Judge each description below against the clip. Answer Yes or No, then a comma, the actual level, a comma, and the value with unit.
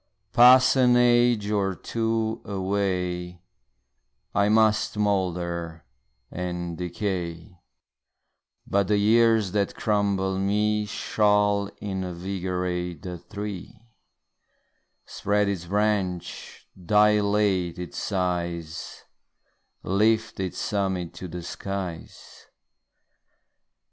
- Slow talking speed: Yes, slow, 85 wpm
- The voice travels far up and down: No, average, 2.8 semitones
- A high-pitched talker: No, low, 100 Hz